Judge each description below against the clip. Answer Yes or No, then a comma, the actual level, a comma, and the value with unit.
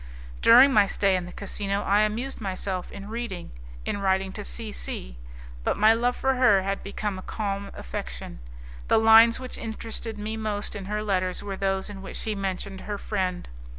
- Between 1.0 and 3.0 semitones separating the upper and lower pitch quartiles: Yes, narrow, 2.4 semitones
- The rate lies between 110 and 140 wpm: No, average, 185 wpm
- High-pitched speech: Yes, high, 205 Hz